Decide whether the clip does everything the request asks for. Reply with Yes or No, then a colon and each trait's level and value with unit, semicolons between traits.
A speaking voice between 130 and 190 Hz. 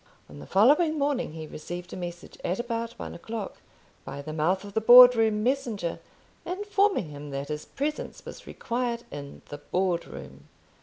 No: high, 205 Hz